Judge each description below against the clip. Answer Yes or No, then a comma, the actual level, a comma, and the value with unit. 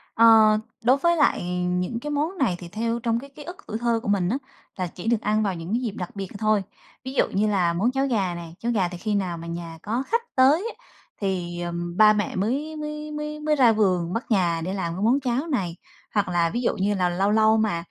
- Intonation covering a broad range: Yes, wide, 6.0 semitones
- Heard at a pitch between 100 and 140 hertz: No, high, 215 Hz